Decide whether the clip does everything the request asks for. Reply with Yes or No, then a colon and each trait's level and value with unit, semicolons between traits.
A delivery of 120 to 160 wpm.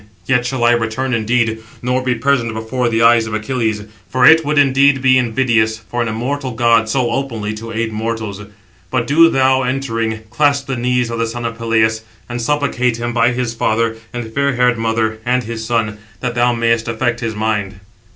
No: average, 195 wpm